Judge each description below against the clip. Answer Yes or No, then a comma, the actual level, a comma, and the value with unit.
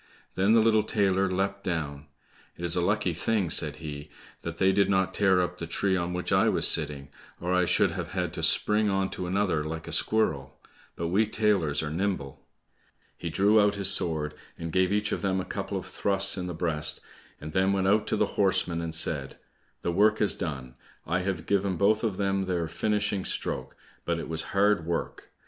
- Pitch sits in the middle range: No, very low, 95 Hz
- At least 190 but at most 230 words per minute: Yes, fast, 205 wpm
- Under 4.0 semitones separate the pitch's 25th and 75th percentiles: Yes, average, 3.3 semitones